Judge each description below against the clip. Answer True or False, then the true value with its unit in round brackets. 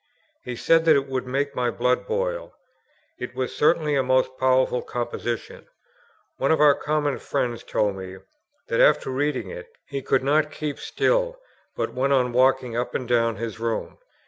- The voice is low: True (130 Hz)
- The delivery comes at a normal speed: True (170 wpm)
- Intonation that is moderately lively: True (3.3 semitones)